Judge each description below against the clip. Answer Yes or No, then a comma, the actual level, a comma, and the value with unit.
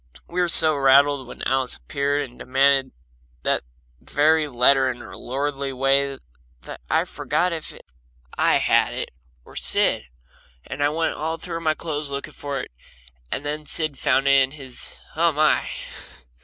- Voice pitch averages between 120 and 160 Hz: Yes, medium, 140 Hz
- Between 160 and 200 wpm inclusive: Yes, average, 165 wpm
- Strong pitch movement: No, narrow, 2.4 semitones